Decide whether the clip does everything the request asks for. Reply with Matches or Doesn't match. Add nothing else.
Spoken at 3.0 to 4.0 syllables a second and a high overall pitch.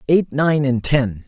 Doesn't match